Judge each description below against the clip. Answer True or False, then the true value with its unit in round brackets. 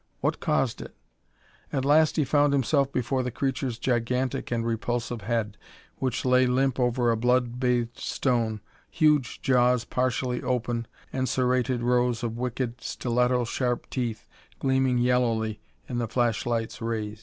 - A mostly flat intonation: True (1.6 semitones)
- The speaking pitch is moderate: False (125 Hz)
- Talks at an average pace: True (145 wpm)